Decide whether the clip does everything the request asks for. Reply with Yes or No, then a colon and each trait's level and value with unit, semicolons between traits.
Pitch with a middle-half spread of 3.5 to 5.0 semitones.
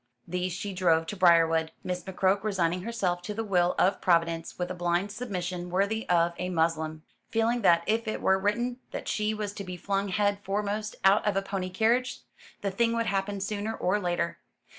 No: average, 2.9 semitones